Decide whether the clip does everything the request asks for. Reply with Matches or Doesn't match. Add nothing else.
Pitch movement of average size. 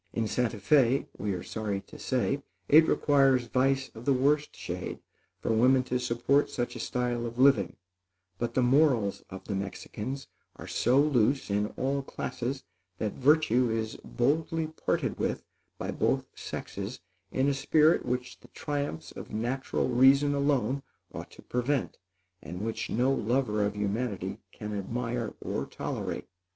Matches